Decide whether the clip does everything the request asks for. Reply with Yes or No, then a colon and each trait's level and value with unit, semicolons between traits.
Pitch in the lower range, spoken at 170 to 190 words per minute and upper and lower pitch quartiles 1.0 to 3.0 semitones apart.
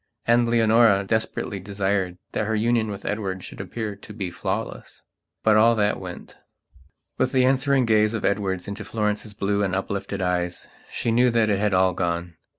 Yes: low, 105 Hz; average, 175 wpm; average, 2.7 semitones